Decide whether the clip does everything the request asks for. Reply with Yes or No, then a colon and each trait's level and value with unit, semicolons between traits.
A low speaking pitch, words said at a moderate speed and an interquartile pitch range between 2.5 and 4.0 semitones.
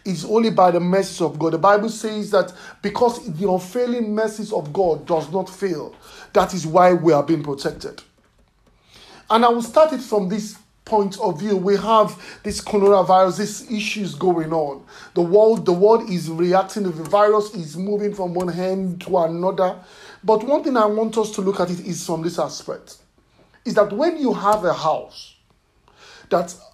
No: high, 200 Hz; average, 185 wpm; average, 3.0 semitones